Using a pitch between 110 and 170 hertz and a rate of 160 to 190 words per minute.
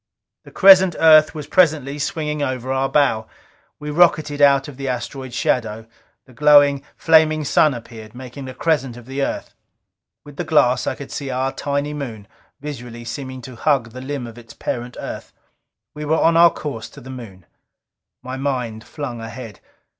Yes: low, 135 Hz; average, 175 wpm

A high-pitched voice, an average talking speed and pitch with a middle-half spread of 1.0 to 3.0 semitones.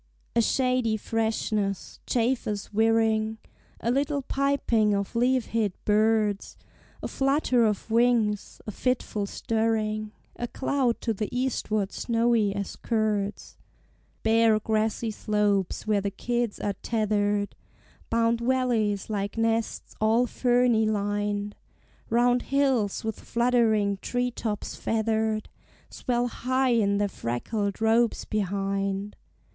No: high, 220 Hz; slow, 115 wpm; narrow, 2.5 semitones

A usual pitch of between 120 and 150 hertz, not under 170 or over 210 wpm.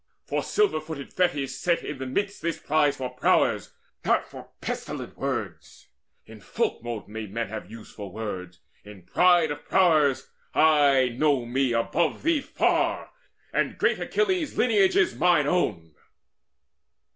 No: medium, 140 Hz; average, 145 wpm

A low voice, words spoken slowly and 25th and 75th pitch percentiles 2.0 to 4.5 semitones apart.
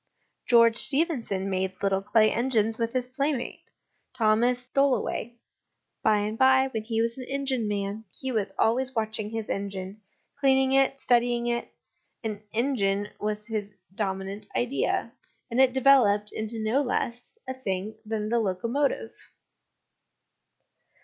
No: high, 230 Hz; slow, 130 wpm; average, 3.7 semitones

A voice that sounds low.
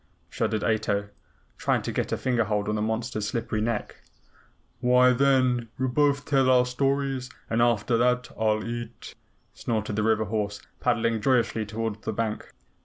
Yes: low, 115 Hz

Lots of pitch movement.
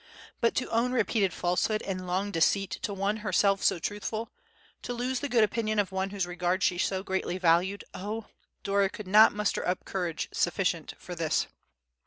No: average, 2.8 semitones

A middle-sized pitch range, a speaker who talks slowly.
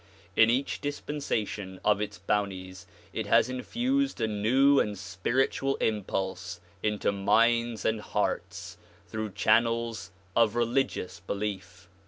Yes: average, 3.5 semitones; slow, 115 wpm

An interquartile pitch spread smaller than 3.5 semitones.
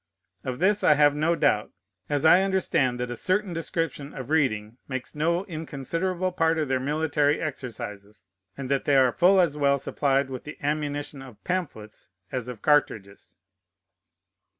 No: average, 4.2 semitones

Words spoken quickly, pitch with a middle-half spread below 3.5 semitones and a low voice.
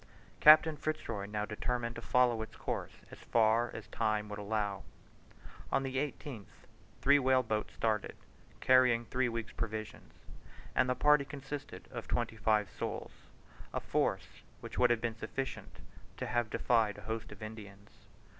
No: average, 155 wpm; average, 3.1 semitones; low, 115 Hz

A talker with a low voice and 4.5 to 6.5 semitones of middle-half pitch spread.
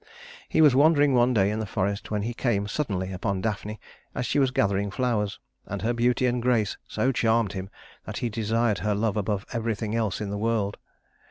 No: low, 110 Hz; average, 2.9 semitones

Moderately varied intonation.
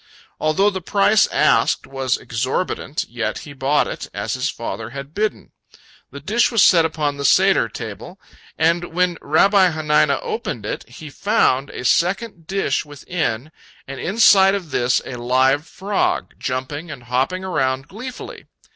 No: wide, 6.3 semitones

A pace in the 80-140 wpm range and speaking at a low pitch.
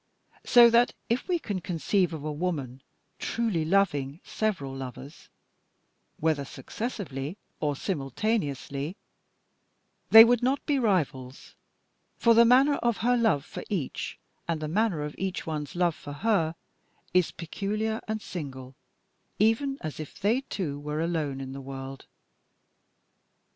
No: slow, 135 wpm; medium, 170 Hz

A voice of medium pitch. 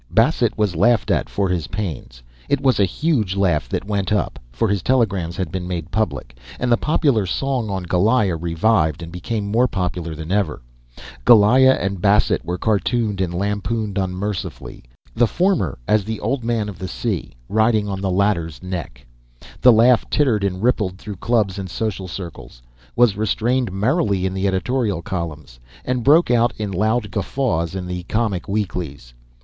No: low, 100 Hz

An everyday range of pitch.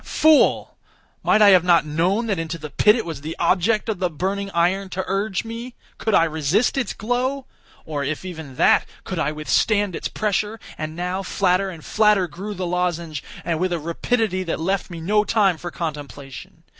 Yes: average, 4.2 semitones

